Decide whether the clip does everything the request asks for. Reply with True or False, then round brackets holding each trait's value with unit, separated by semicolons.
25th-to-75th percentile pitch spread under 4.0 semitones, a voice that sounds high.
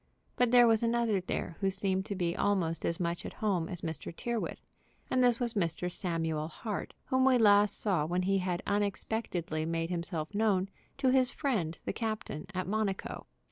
False (4.7 semitones; 195 Hz)